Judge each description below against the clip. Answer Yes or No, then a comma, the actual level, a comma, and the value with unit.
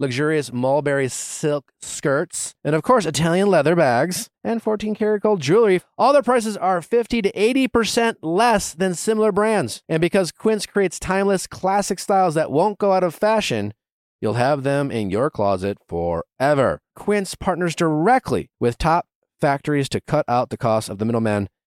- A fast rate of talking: No, average, 165 wpm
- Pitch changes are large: Yes, wide, 7.1 semitones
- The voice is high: No, medium, 175 Hz